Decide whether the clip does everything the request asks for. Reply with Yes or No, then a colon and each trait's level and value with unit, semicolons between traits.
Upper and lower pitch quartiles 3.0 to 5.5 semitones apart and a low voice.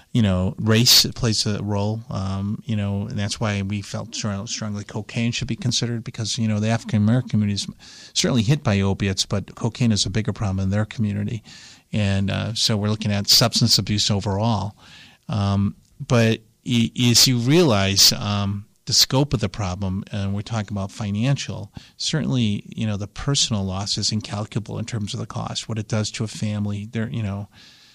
No: narrow, 2.4 semitones; low, 110 Hz